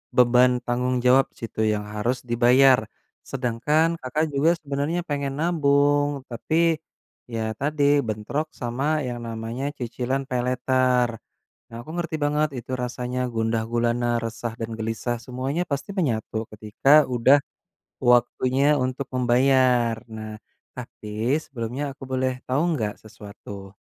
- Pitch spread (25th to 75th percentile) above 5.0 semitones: No, average, 3.4 semitones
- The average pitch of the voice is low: Yes, low, 125 Hz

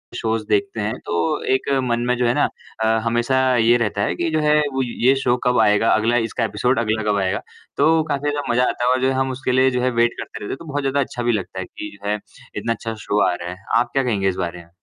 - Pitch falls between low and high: No, low, 120 Hz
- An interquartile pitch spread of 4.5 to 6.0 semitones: No, average, 3.3 semitones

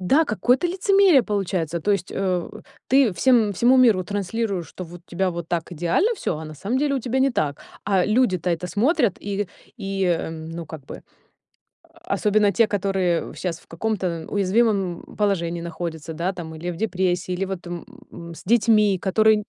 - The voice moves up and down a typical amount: Yes, average, 4.2 semitones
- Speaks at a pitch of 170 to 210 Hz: Yes, high, 190 Hz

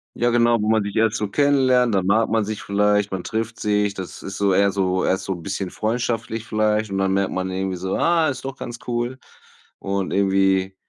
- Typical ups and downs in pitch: Yes, average, 3.1 semitones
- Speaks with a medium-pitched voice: No, low, 105 Hz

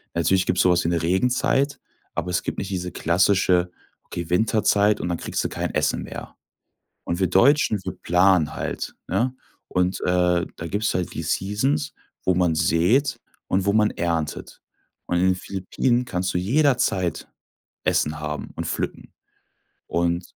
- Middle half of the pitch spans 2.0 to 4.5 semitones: Yes, average, 2.9 semitones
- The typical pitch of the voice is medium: No, very low, 90 Hz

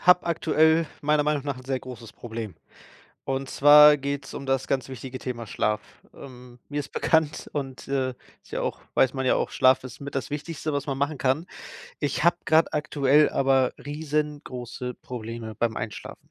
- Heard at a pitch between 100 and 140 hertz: Yes, low, 135 Hz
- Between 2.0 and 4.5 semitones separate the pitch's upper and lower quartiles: Yes, average, 2.7 semitones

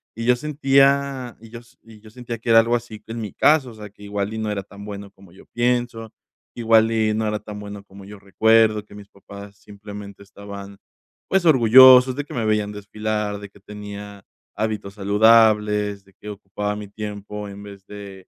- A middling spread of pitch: No, narrow, 2.1 semitones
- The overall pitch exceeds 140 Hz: No, low, 105 Hz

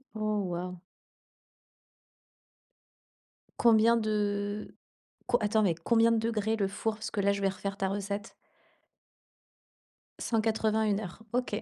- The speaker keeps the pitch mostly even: Yes, narrow, 1.8 semitones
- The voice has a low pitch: No, high, 210 Hz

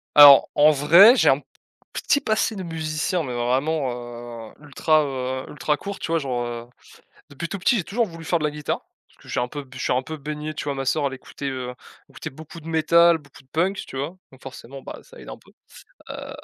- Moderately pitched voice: Yes, medium, 150 Hz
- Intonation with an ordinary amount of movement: Yes, average, 3.7 semitones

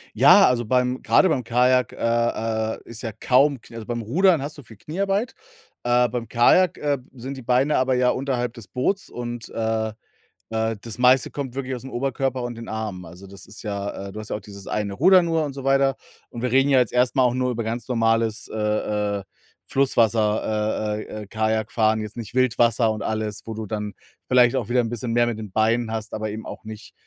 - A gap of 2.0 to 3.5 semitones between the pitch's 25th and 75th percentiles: Yes, average, 2.8 semitones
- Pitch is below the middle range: Yes, low, 120 Hz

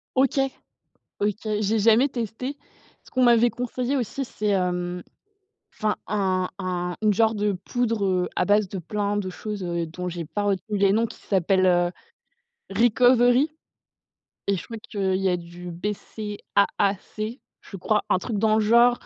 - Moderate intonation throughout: Yes, average, 3.5 semitones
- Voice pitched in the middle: No, high, 205 Hz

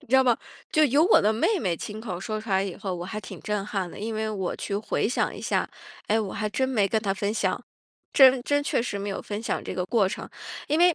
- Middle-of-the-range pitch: No, high, 215 Hz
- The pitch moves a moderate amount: Yes, average, 3.7 semitones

